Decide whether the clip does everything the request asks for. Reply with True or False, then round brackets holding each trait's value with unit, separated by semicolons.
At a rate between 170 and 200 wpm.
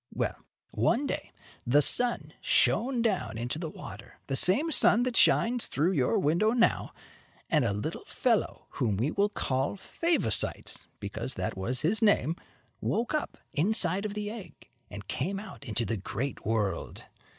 False (160 wpm)